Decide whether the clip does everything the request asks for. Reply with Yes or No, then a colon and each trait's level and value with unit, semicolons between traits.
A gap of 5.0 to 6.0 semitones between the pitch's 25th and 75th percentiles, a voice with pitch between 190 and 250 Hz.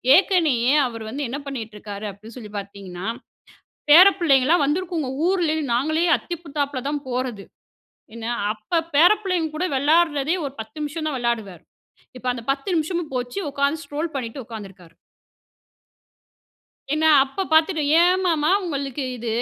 No: wide, 5.6 semitones; very high, 280 Hz